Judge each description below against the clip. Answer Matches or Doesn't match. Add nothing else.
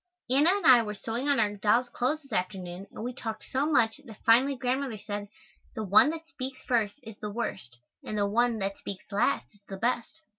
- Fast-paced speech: Matches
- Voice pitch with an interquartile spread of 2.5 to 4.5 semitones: Matches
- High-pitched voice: Matches